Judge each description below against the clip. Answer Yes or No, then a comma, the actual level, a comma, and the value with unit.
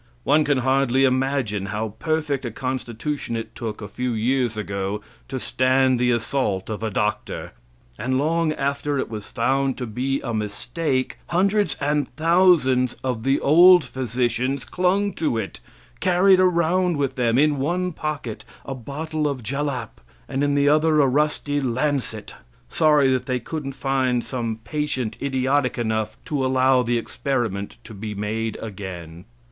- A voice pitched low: Yes, low, 130 Hz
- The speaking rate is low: No, average, 155 wpm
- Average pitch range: Yes, average, 4.2 semitones